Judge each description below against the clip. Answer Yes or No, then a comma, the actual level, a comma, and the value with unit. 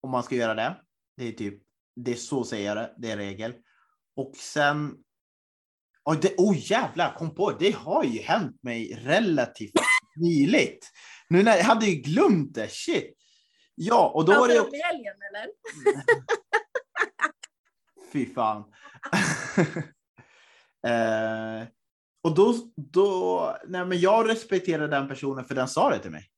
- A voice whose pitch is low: No, medium, 160 Hz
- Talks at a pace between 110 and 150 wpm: Yes, average, 145 wpm